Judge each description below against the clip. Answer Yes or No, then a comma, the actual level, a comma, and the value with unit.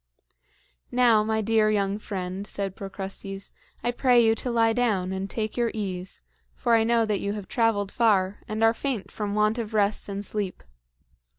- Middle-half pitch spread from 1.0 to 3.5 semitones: Yes, narrow, 2.4 semitones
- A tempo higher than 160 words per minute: Yes, average, 180 wpm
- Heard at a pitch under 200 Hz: No, high, 215 Hz